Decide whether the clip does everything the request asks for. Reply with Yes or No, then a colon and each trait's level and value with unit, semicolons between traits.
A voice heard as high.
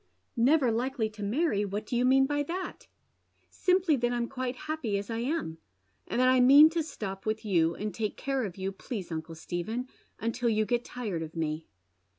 Yes: high, 235 Hz